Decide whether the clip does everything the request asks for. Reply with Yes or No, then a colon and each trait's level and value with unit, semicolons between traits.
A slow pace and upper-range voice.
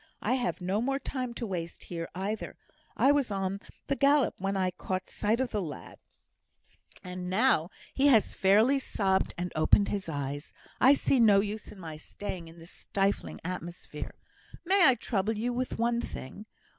No: average, 175 wpm; high, 200 Hz